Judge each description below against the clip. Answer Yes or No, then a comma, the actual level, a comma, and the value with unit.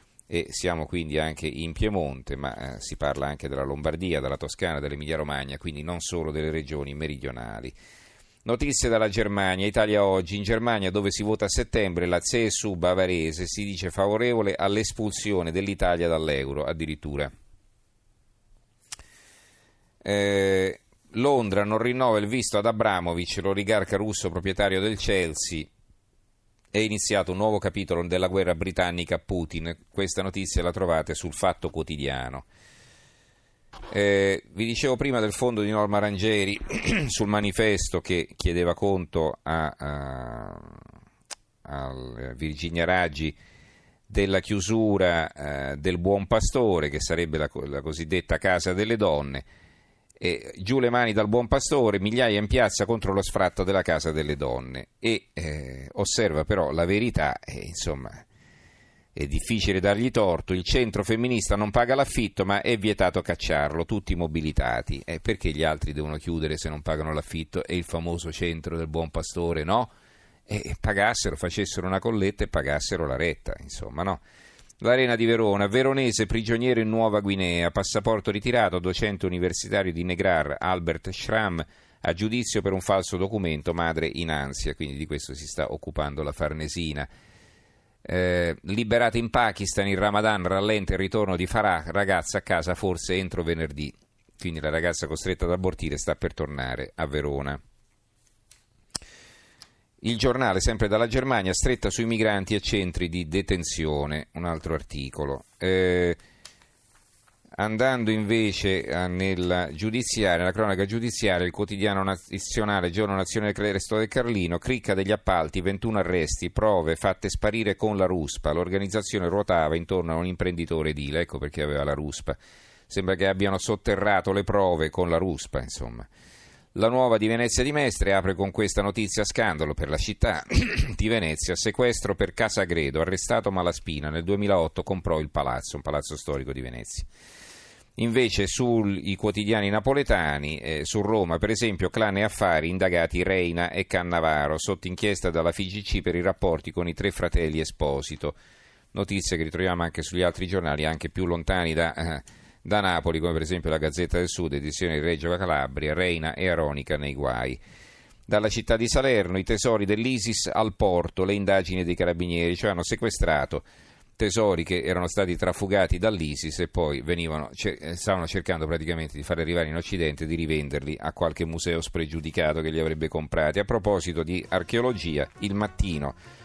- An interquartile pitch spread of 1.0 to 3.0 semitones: No, average, 4.6 semitones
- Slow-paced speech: No, average, 150 wpm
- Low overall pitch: Yes, very low, 90 Hz